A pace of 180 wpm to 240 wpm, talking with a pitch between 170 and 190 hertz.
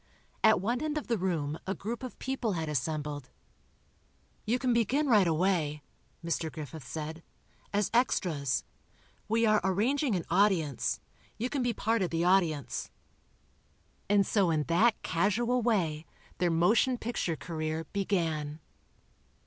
No: average, 140 wpm; medium, 185 Hz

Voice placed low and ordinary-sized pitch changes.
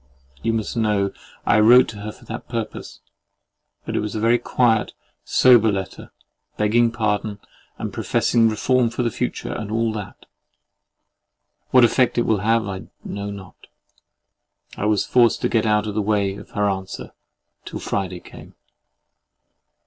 No: low, 110 Hz; narrow, 2.2 semitones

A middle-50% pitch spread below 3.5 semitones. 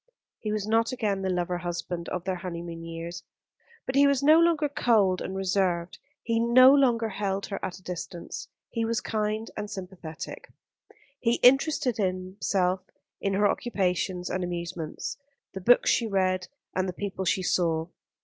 No: average, 4.0 semitones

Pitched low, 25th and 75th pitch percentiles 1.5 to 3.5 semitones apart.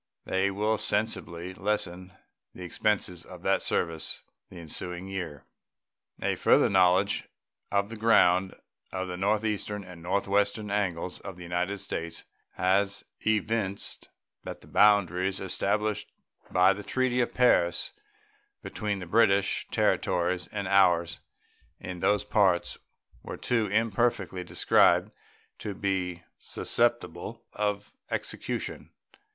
Yes: very low, 95 Hz; narrow, 2.6 semitones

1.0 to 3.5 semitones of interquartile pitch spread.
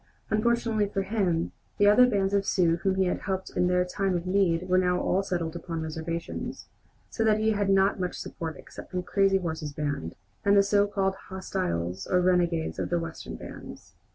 Yes: average, 3.0 semitones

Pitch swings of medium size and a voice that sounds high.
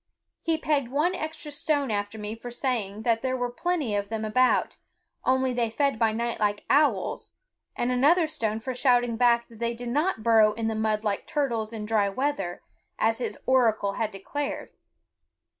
Yes: average, 3.7 semitones; high, 235 Hz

